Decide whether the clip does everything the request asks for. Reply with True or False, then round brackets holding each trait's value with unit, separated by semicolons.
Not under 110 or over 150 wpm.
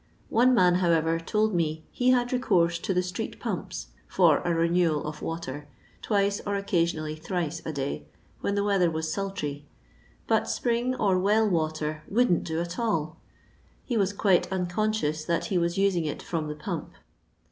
False (175 wpm)